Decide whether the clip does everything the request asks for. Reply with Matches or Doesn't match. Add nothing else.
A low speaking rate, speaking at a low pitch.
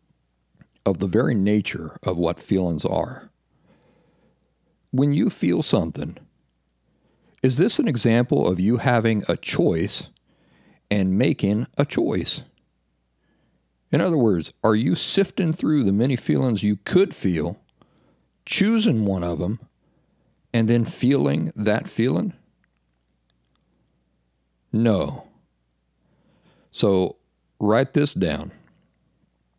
Matches